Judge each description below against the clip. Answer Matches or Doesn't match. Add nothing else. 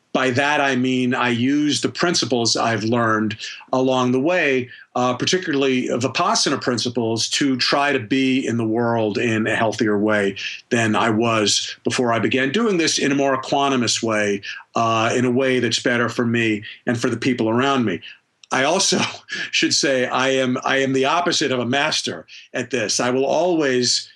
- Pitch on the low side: Matches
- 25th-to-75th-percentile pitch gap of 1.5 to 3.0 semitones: Matches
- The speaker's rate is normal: Matches